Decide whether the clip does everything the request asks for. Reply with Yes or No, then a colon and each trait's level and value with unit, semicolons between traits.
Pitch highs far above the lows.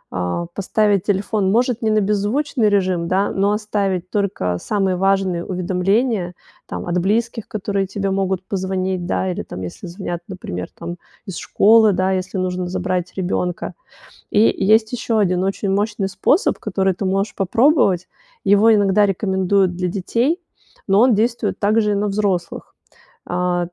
No: narrow, 2.4 semitones